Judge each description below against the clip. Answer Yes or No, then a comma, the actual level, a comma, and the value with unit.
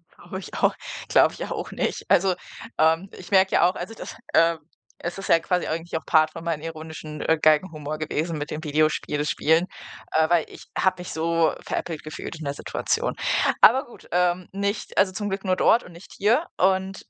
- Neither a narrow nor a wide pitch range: Yes, average, 3.2 semitones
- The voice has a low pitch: No, medium, 170 Hz